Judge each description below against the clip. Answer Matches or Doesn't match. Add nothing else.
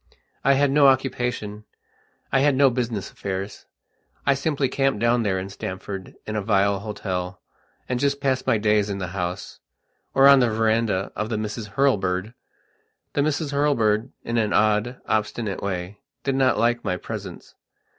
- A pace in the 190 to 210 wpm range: Doesn't match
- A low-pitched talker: Matches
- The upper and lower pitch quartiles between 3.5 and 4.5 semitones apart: Doesn't match